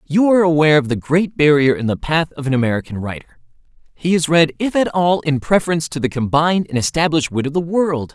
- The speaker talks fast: Yes, fast, 230 wpm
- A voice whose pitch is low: No, medium, 155 Hz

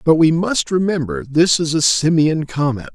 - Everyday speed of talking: Yes, average, 185 wpm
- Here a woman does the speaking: No, male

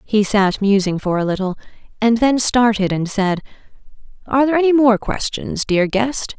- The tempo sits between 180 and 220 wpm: No, average, 170 wpm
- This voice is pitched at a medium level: No, high, 220 Hz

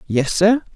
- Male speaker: Yes, male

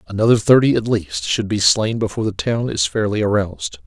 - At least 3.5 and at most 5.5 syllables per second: No, 5.7 syllables/s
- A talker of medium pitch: No, low, 105 Hz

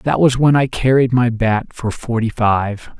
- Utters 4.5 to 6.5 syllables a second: No, 4.1 syllables/s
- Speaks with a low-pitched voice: Yes, low, 120 Hz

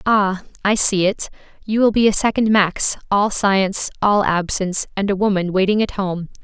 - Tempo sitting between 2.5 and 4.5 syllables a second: No, 4.9 syllables/s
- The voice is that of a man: No, female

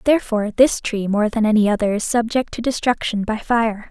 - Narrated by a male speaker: No, female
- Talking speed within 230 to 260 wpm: No, average, 200 wpm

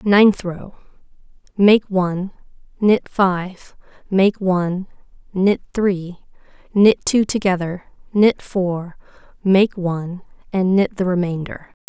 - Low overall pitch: No, high, 190 Hz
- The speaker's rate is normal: No, slow, 100 wpm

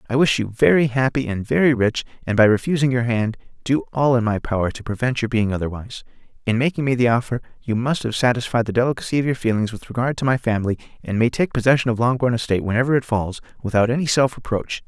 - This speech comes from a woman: No, male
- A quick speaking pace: Yes, fast, 225 wpm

